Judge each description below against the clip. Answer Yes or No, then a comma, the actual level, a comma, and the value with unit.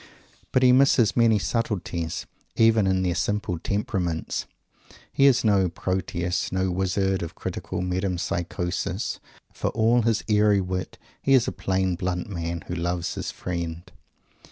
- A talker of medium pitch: No, very low, 95 Hz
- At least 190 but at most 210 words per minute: No, average, 140 wpm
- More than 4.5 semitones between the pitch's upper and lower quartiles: No, average, 3.4 semitones